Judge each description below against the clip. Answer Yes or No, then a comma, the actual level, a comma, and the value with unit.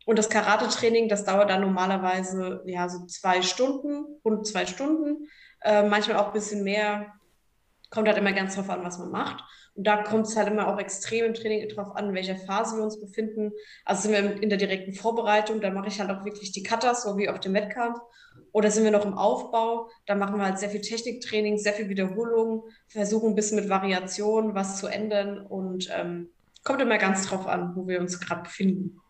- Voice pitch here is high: Yes, high, 205 Hz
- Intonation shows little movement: Yes, narrow, 2.1 semitones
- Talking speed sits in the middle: No, fast, 210 wpm